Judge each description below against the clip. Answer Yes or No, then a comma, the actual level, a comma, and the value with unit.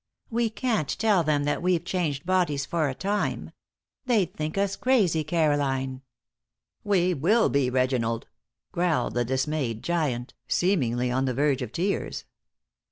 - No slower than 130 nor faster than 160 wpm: Yes, average, 140 wpm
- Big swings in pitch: Yes, wide, 5.8 semitones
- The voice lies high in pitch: No, medium, 155 Hz